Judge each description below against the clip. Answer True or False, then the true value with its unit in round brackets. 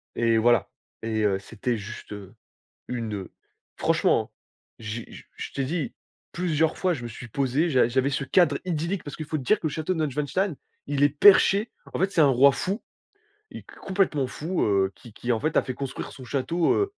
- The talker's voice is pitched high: False (140 Hz)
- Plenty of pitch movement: True (5.7 semitones)